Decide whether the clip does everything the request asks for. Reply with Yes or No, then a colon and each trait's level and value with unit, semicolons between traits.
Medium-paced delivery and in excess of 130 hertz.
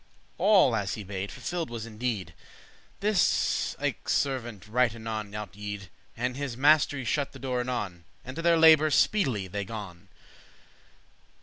No: average, 165 wpm; low, 120 Hz